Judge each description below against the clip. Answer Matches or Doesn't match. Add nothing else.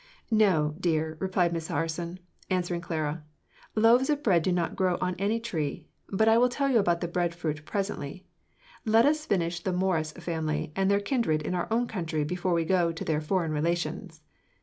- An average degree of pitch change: Matches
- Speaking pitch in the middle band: Matches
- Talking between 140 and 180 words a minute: Doesn't match